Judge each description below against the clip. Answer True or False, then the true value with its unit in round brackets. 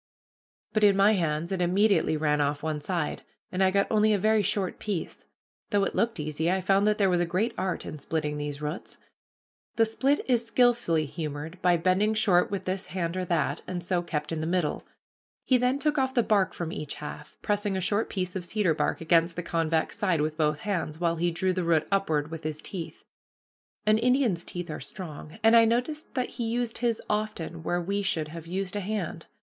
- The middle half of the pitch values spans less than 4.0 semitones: False (4.5 semitones)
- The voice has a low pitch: False (185 Hz)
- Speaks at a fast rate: True (215 wpm)